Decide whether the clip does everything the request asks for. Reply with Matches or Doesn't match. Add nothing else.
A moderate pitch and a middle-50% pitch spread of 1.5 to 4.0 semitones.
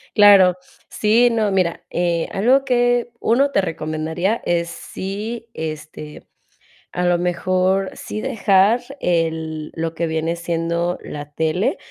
Doesn't match